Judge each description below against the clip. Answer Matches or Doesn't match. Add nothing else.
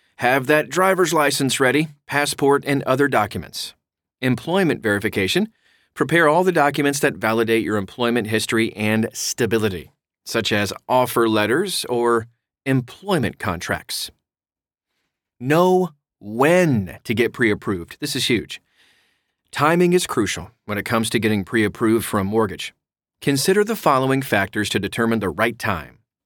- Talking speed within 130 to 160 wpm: Matches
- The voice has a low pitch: Matches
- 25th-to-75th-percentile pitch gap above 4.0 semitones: Matches